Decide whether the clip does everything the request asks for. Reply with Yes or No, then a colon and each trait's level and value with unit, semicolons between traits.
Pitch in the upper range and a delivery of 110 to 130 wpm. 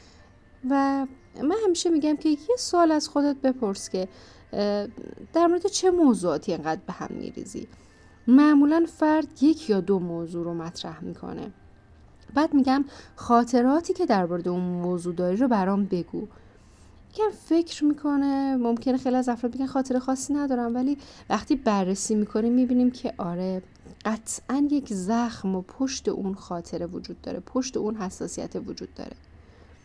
No: very high, 250 Hz; average, 145 wpm